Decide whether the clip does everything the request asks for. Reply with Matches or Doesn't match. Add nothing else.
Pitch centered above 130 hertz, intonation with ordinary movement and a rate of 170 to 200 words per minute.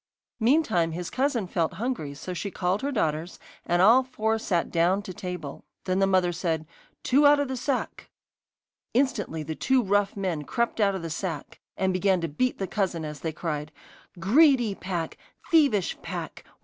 Doesn't match